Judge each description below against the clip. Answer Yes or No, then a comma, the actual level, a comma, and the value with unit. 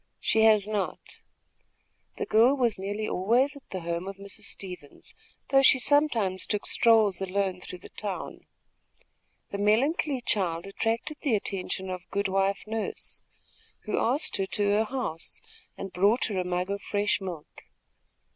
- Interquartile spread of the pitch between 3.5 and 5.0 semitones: No, average, 3.1 semitones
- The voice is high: Yes, high, 205 Hz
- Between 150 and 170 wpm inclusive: Yes, average, 155 wpm